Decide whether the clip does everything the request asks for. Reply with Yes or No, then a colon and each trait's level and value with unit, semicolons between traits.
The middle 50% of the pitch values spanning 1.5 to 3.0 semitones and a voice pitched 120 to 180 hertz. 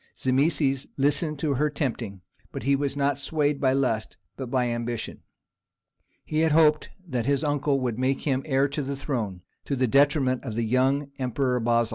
Yes: narrow, 2.5 semitones; low, 135 Hz